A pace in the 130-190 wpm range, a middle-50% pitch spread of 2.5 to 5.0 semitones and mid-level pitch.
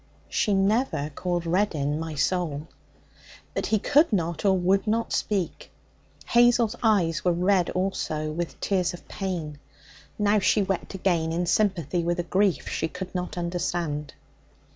Yes: average, 145 wpm; average, 3.2 semitones; medium, 180 Hz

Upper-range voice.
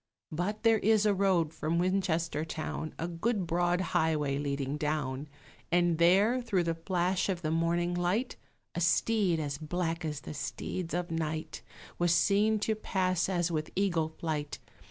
No: medium, 175 Hz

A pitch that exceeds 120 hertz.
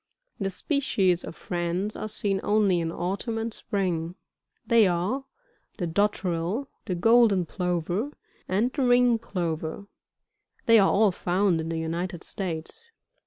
Yes: high, 190 Hz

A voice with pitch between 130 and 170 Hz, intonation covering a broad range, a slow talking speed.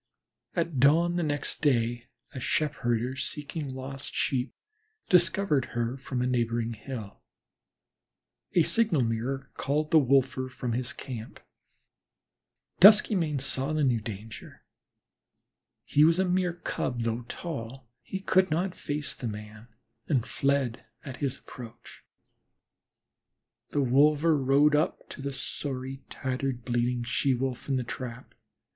No: low, 135 Hz; average, 3.8 semitones; slow, 130 wpm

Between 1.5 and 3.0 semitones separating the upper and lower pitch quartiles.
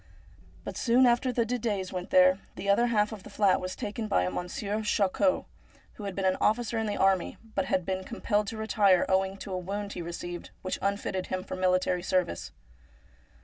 Yes: average, 2.7 semitones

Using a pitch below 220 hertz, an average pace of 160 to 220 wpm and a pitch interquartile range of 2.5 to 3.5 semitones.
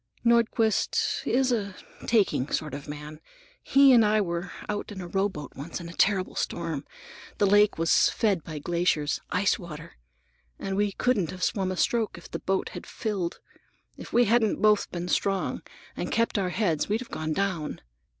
No: high, 190 Hz; average, 170 wpm; average, 4.3 semitones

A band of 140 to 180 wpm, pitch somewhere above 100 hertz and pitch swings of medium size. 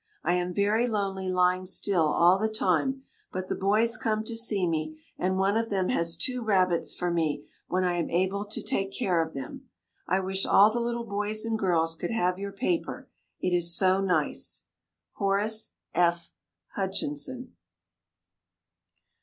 Yes: average, 165 wpm; high, 190 Hz; average, 3.5 semitones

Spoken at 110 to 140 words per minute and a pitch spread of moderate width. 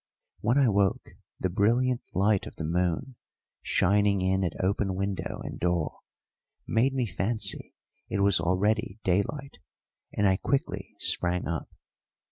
Yes: slow, 135 wpm; average, 3.4 semitones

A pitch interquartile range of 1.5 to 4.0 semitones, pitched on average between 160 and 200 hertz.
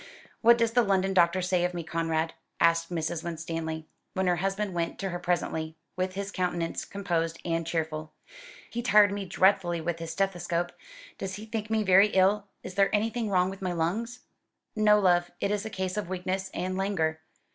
Yes: average, 3.0 semitones; medium, 185 Hz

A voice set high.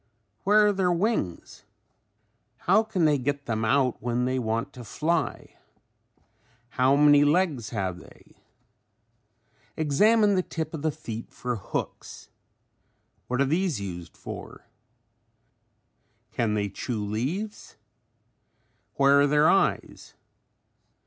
No: medium, 140 Hz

